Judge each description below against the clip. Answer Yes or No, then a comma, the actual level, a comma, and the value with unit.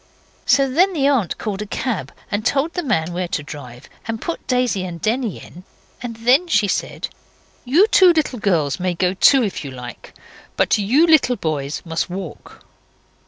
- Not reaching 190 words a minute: Yes, average, 180 wpm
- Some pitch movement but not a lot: No, wide, 7.9 semitones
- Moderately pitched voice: No, high, 215 Hz